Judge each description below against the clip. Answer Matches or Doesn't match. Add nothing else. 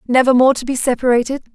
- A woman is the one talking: Matches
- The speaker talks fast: Doesn't match